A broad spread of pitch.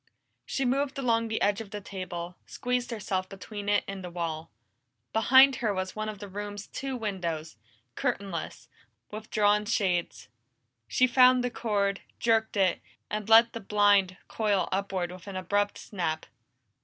No: average, 3.3 semitones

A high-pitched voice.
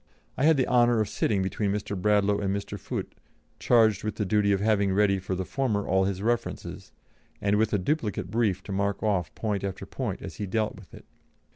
No: low, 100 Hz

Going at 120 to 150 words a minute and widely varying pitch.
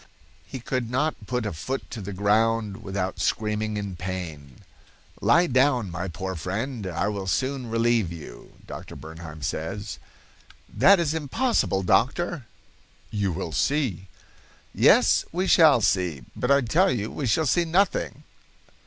Yes: average, 145 wpm; wide, 6.3 semitones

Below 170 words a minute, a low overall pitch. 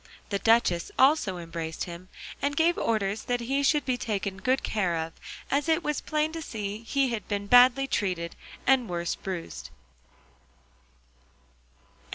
No: average, 150 wpm; high, 225 Hz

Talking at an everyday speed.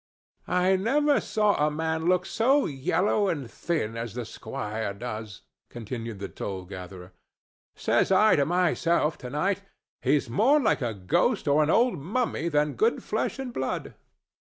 Yes: average, 150 wpm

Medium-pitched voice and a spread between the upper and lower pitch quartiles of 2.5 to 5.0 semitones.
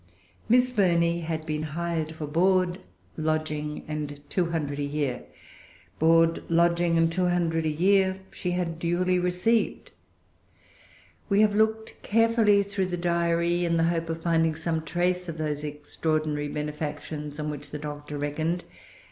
Yes: medium, 165 Hz; average, 2.8 semitones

